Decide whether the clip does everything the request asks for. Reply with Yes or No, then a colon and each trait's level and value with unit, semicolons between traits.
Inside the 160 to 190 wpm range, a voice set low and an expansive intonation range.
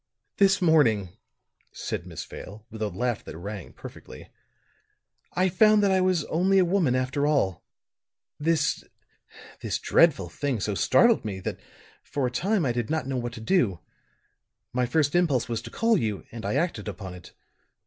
Yes: average, 170 wpm; low, 130 Hz; wide, 8.4 semitones